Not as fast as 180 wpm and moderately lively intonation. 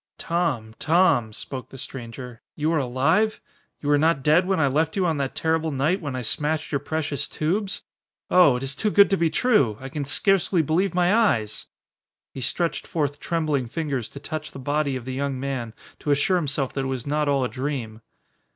No: fast, 205 wpm; average, 3.7 semitones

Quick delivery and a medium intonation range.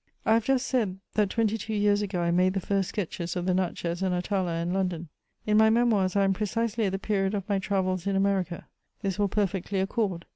No: fast, 225 wpm; narrow, 2.3 semitones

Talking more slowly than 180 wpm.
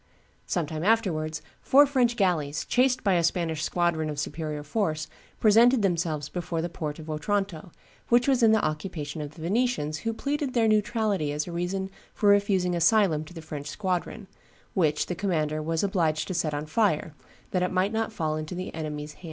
No: average, 190 wpm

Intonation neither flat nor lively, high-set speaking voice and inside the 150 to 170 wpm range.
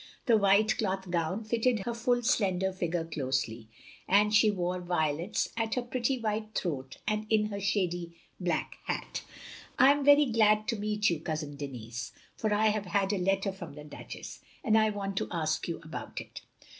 No: average, 4.4 semitones; high, 195 Hz; average, 180 wpm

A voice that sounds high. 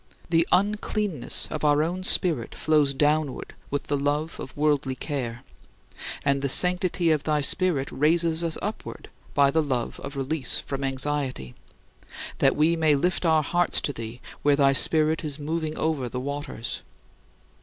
No: medium, 150 Hz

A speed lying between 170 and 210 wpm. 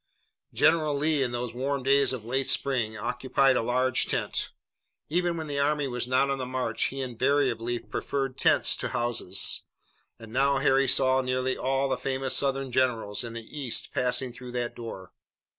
Yes: average, 175 wpm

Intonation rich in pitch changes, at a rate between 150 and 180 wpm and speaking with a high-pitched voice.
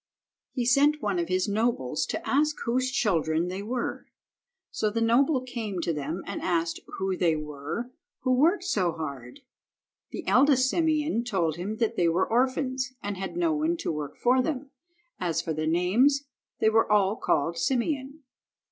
Yes: wide, 7.3 semitones; average, 170 wpm; high, 225 Hz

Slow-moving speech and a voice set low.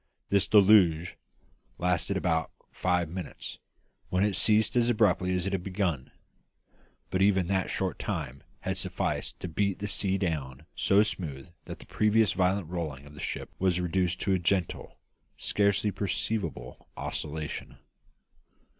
No: average, 145 wpm; very low, 90 Hz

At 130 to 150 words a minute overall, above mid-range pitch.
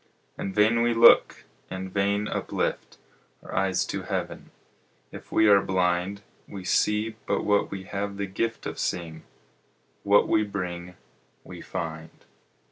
No: average, 140 wpm; low, 100 Hz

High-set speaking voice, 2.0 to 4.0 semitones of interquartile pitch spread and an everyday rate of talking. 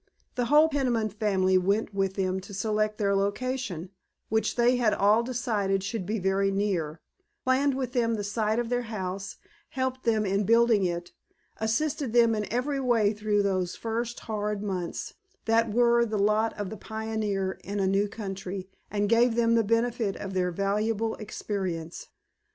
Yes: high, 215 Hz; average, 2.9 semitones; average, 170 wpm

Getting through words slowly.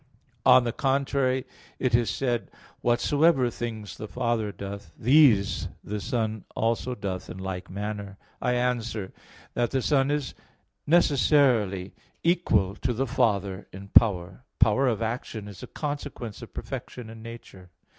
No: average, 145 wpm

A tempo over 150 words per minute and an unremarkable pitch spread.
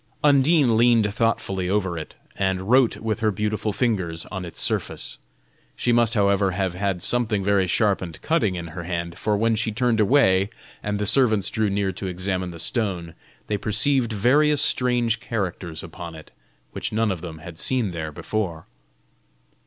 Yes: average, 170 wpm; average, 4.0 semitones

